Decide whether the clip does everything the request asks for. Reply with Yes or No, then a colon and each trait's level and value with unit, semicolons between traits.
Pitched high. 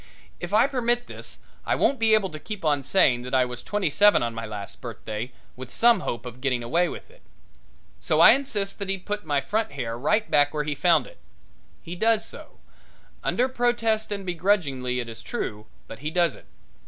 No: medium, 175 Hz